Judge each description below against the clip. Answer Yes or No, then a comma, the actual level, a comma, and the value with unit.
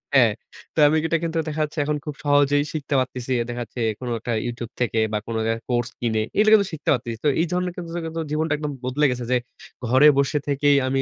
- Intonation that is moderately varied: Yes, average, 4.2 semitones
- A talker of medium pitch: Yes, medium, 145 Hz